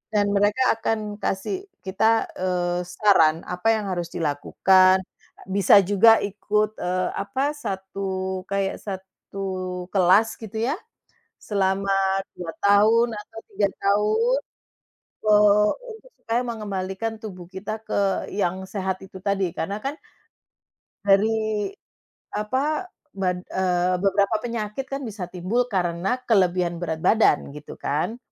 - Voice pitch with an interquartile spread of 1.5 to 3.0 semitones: Yes, average, 2.7 semitones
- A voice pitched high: Yes, high, 200 Hz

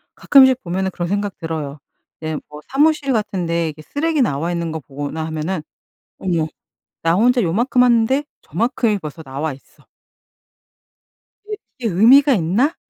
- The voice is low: No, medium, 185 Hz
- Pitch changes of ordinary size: No, wide, 7.7 semitones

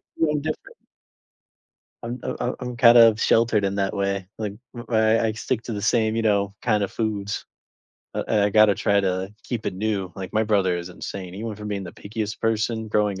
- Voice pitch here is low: Yes, low, 105 Hz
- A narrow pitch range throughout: Yes, narrow, 2.3 semitones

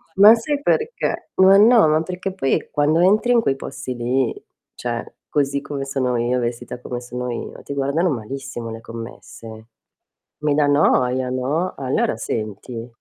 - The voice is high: No, low, 135 Hz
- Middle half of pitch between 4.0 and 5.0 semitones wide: Yes, average, 4.6 semitones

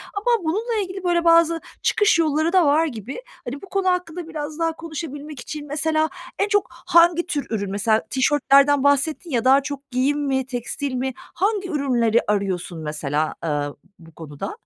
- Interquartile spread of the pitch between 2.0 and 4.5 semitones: No, average, 5.2 semitones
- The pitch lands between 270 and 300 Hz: Yes, very high, 290 Hz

